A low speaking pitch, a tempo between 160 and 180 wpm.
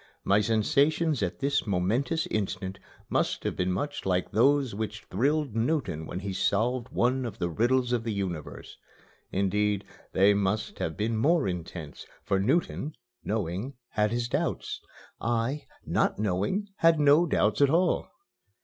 No: low, 110 Hz; average, 150 wpm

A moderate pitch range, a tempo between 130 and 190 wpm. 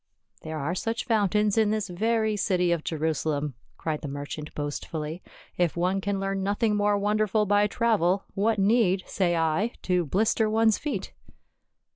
Yes: average, 4.3 semitones; average, 170 wpm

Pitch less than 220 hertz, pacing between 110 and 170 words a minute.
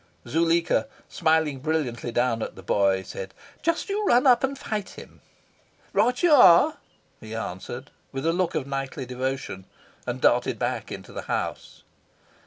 Yes: medium, 140 Hz; average, 155 wpm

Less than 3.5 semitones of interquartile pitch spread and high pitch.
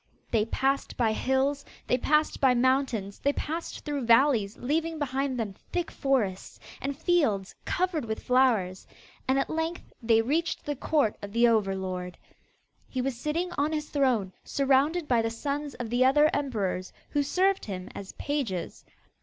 No: average, 4.7 semitones; very high, 265 Hz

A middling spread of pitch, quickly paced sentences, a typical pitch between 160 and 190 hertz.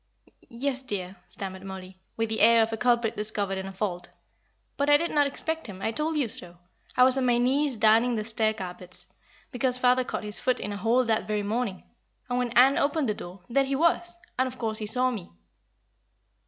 No: average, 3.9 semitones; fast, 215 wpm; high, 230 Hz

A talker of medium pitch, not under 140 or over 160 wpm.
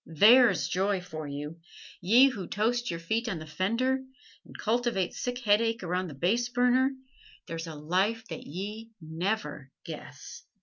No: high, 200 Hz; average, 150 wpm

